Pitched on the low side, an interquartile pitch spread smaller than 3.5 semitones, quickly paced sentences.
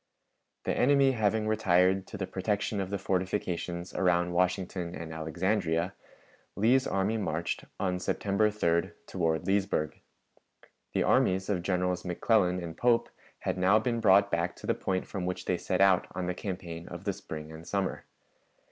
No: very low, 95 Hz; narrow, 2.5 semitones; average, 160 wpm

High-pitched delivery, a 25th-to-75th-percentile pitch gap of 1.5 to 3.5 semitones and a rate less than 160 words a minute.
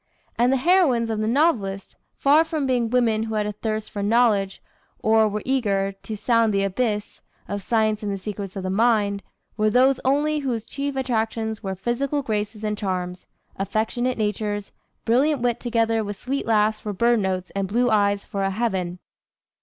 No: high, 220 Hz; average, 3.2 semitones; average, 180 wpm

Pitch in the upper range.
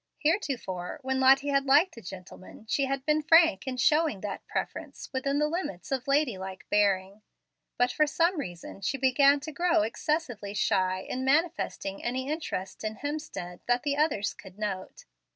Yes: very high, 265 Hz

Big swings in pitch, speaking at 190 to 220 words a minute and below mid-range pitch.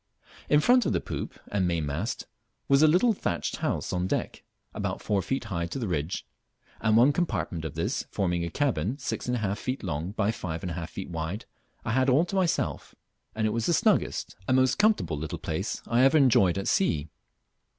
Yes: wide, 7.8 semitones; fast, 205 wpm; low, 105 Hz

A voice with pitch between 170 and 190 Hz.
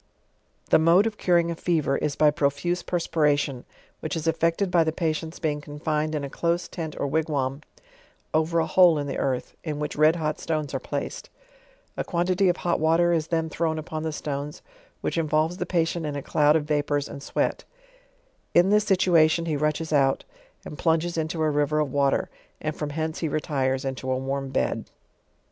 No: medium, 155 Hz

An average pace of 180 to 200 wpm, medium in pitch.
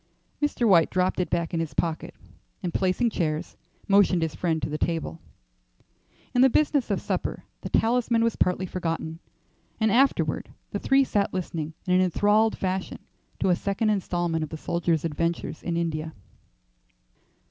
No: average, 160 wpm; medium, 180 Hz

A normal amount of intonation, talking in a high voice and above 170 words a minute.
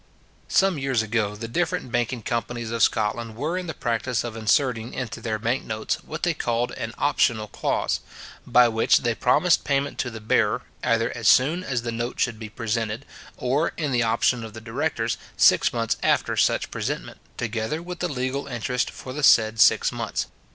No: average, 3.1 semitones; low, 120 Hz; average, 185 wpm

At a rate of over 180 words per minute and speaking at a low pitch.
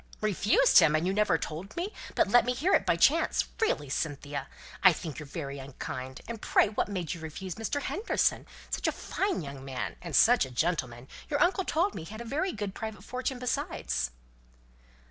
No: average, 200 wpm; high, 190 Hz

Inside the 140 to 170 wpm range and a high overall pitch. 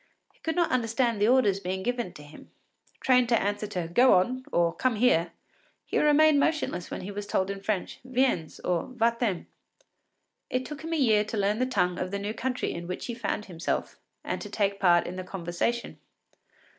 No: average, 195 wpm; high, 210 Hz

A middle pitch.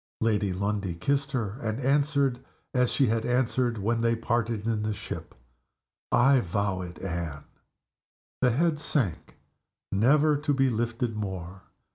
No: low, 115 Hz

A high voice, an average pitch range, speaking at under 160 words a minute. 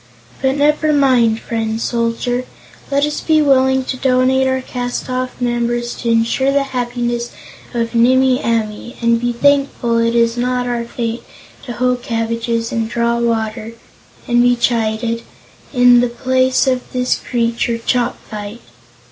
No: high, 240 Hz; narrow, 1.8 semitones; average, 145 wpm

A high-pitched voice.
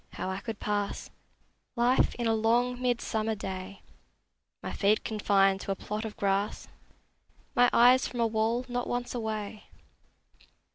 Yes: high, 220 Hz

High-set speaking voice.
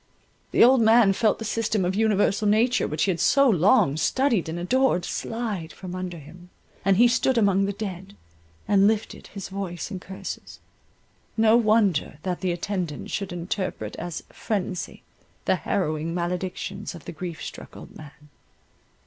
Yes: high, 195 Hz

